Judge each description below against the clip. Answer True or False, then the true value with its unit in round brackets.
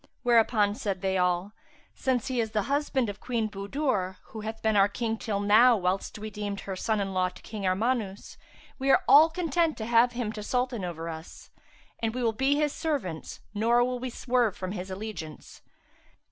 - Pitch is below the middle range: False (220 Hz)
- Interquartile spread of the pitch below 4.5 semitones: True (4.1 semitones)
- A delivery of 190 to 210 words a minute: True (195 wpm)